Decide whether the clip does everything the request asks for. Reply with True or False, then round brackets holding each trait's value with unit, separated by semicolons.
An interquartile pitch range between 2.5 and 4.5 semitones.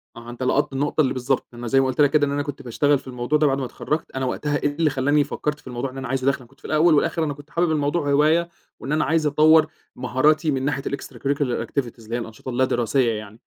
True (2.8 semitones)